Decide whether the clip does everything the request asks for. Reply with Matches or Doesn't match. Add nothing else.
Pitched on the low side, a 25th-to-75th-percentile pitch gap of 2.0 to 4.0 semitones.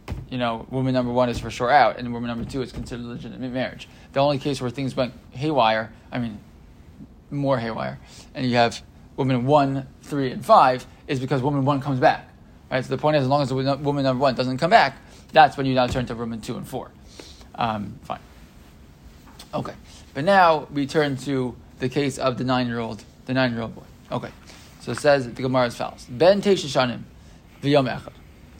Matches